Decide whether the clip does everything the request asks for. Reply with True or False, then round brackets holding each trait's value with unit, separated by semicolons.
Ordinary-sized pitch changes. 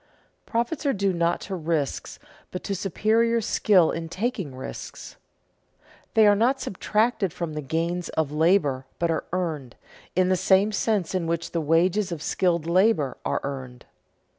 True (4.2 semitones)